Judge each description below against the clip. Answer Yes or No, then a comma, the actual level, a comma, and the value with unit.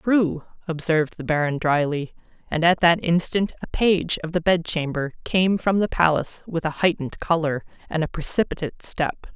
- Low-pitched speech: No, medium, 165 Hz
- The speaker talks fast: No, average, 165 wpm